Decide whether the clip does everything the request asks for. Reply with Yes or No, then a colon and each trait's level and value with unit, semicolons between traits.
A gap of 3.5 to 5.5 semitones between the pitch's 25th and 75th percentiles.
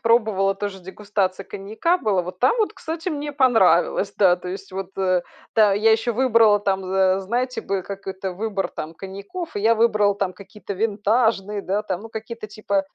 No: average, 2.8 semitones